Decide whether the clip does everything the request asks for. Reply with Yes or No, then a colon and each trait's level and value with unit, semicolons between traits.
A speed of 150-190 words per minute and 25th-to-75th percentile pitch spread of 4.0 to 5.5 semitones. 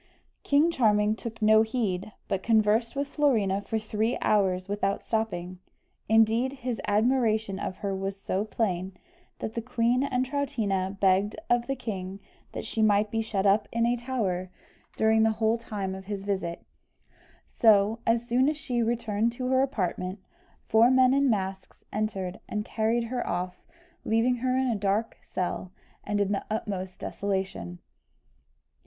No: average, 160 wpm; average, 3.4 semitones